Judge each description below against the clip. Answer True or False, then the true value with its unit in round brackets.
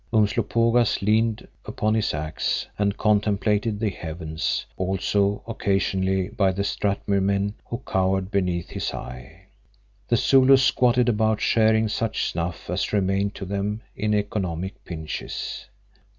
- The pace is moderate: False (120 wpm)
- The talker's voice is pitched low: True (100 Hz)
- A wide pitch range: False (2.6 semitones)